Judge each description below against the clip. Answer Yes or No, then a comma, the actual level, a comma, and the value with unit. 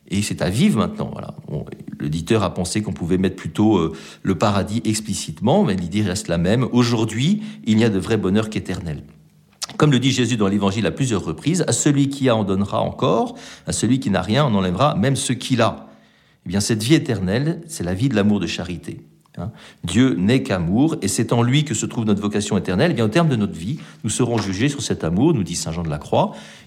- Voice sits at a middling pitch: No, low, 110 Hz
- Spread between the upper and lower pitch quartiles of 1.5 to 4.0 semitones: No, average, 4.6 semitones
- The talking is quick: Yes, fast, 230 wpm